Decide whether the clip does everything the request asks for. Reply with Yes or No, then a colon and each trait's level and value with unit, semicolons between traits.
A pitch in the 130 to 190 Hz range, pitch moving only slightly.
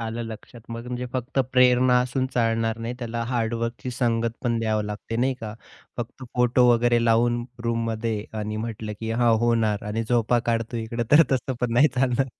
No: low, 115 Hz; narrow, 1.5 semitones